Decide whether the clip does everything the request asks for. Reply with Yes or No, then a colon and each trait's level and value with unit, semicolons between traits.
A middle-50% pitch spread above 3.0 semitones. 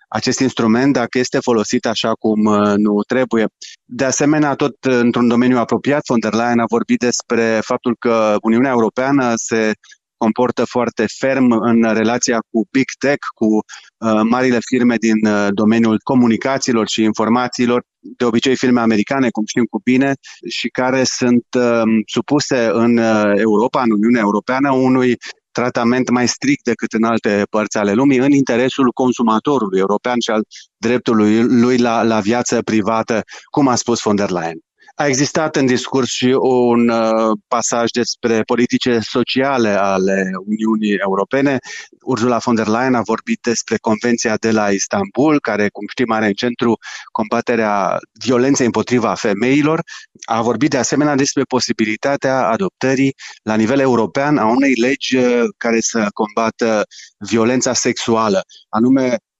No: narrow, 2.5 semitones